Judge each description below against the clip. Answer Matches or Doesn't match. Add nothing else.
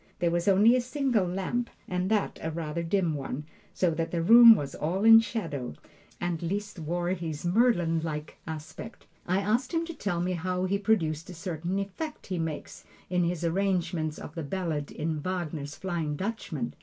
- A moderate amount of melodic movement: Matches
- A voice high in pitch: Doesn't match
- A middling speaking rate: Matches